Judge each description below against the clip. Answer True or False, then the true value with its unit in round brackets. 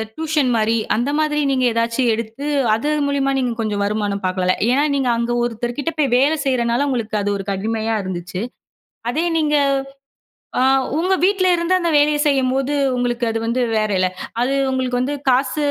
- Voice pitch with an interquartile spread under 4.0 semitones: False (4.4 semitones)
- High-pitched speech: True (250 Hz)